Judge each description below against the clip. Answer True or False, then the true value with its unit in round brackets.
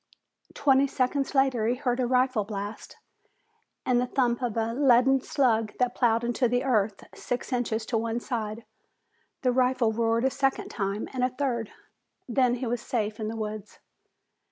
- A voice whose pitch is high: True (245 Hz)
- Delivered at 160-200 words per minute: True (170 wpm)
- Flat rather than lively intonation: True (2.3 semitones)